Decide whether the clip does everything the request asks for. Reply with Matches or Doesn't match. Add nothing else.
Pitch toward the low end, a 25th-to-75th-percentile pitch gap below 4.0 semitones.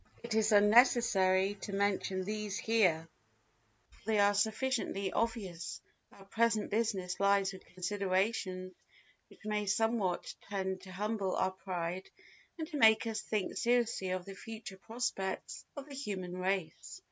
Doesn't match